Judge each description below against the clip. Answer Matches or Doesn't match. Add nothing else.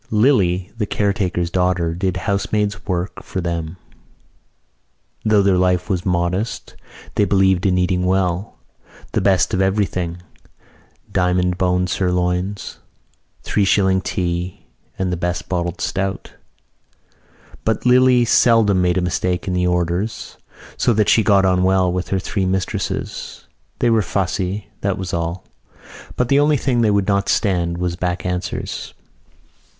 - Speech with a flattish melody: Matches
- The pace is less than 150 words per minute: Matches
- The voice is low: Matches